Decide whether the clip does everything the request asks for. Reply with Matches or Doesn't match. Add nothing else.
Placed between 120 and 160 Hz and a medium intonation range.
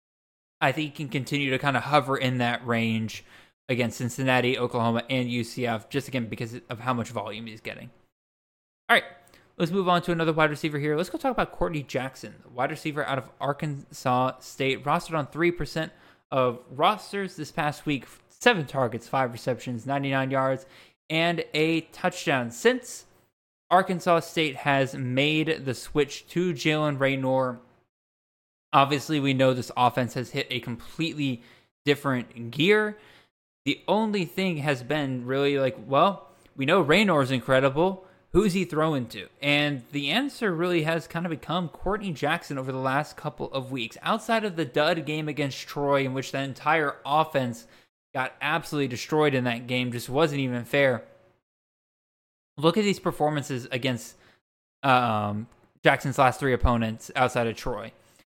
Matches